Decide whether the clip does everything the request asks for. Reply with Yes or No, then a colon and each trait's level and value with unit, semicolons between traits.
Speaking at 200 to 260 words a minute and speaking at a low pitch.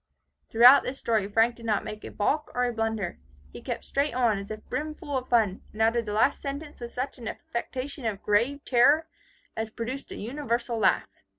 No: fast, 205 wpm; high, 235 Hz